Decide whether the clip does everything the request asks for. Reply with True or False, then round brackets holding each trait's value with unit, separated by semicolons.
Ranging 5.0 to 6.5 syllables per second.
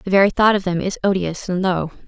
True (5.9 syllables/s)